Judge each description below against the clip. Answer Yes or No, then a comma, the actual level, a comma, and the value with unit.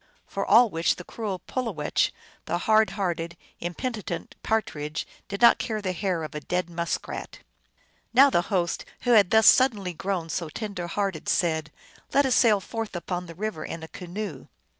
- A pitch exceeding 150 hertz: Yes, medium, 185 Hz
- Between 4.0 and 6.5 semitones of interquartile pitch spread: Yes, average, 4.3 semitones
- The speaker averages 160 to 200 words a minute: Yes, average, 180 wpm